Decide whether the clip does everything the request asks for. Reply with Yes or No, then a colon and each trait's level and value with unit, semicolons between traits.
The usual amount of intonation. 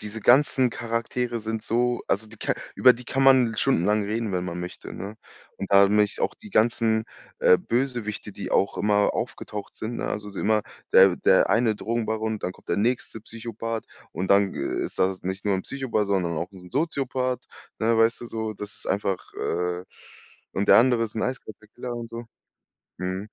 Yes: average, 3.1 semitones